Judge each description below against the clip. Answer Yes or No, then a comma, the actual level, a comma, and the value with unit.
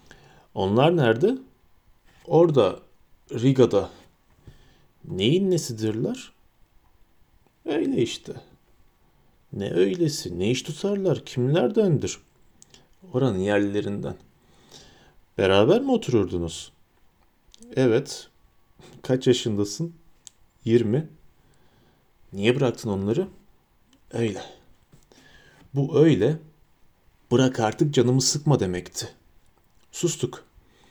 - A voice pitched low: Yes, low, 125 Hz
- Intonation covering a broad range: Yes, wide, 7.1 semitones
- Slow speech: Yes, slow, 70 wpm